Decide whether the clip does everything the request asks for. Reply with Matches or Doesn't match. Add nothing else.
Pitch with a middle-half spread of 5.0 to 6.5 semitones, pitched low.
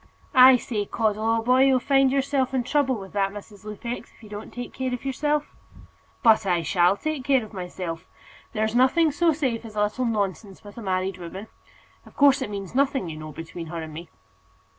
Doesn't match